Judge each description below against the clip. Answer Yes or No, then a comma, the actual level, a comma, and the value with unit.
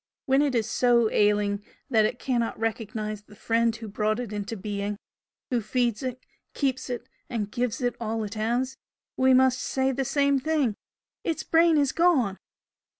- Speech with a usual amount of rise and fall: Yes, average, 3.5 semitones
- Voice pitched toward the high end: Yes, high, 235 Hz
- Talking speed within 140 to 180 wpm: Yes, average, 170 wpm